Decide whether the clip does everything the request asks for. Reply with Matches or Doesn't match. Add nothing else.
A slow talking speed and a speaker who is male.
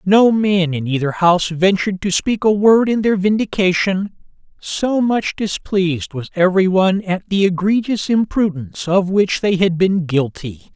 Doesn't match